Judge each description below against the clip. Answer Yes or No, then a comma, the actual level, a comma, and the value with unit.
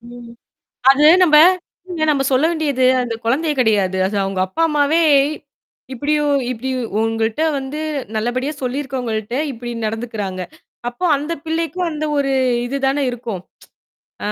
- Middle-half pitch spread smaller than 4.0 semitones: No, average, 4.7 semitones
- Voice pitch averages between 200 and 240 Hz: No, very high, 255 Hz